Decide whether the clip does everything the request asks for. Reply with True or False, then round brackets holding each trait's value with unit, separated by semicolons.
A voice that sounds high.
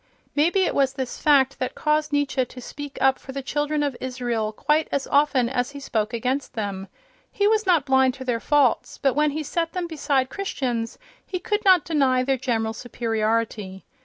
True (270 Hz)